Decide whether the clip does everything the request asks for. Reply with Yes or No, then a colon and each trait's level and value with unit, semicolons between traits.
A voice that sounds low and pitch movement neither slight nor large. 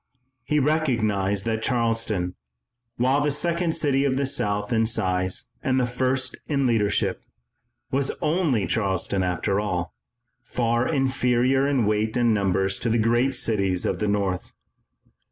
Yes: low, 115 Hz; average, 4.6 semitones